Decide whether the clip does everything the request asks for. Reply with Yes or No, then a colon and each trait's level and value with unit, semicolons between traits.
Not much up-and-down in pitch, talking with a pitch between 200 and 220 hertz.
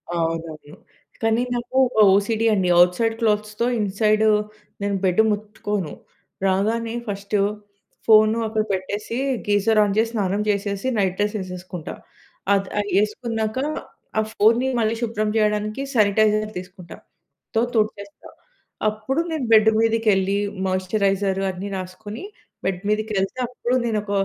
Yes: narrow, 2.1 semitones; high, 210 Hz